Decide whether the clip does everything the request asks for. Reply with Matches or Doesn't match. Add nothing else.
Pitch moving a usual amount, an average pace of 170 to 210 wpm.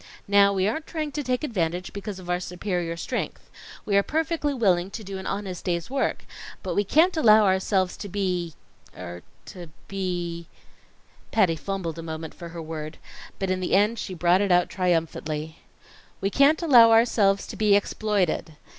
Matches